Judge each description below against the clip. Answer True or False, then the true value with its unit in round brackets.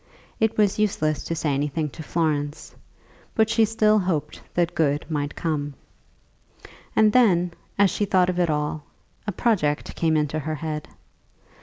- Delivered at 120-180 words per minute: True (155 wpm)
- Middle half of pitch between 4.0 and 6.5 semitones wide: True (5.3 semitones)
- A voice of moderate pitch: True (165 Hz)